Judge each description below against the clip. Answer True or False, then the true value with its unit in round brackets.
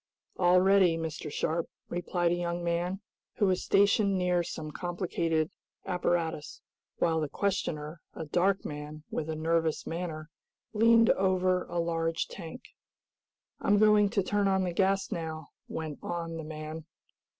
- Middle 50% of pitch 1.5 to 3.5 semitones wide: True (2.8 semitones)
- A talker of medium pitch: True (170 Hz)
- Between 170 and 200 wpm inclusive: False (145 wpm)